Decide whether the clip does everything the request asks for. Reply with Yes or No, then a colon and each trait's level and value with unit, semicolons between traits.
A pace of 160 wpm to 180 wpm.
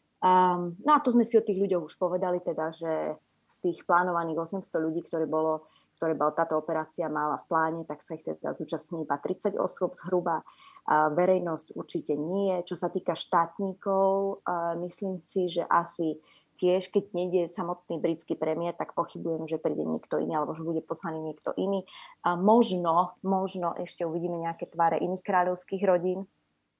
Yes: fast, 165 wpm